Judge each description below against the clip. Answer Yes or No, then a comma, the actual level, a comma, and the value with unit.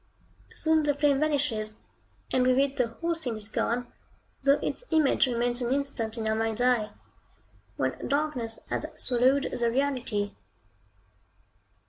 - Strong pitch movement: No, average, 3.6 semitones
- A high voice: Yes, very high, 250 Hz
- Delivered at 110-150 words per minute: Yes, average, 140 wpm